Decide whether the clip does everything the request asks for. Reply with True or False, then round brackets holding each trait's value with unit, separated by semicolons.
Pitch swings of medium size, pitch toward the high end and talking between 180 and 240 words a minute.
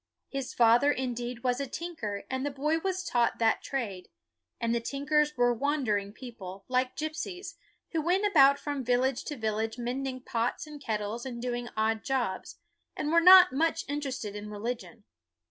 False (4.1 semitones; 255 Hz; 165 wpm)